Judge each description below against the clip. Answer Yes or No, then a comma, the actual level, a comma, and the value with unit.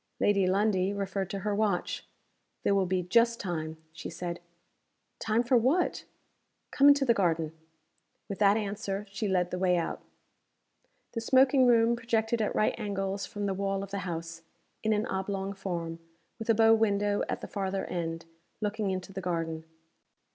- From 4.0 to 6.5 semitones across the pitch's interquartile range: No, average, 3.2 semitones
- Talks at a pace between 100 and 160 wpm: No, average, 170 wpm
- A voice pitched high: Yes, high, 200 Hz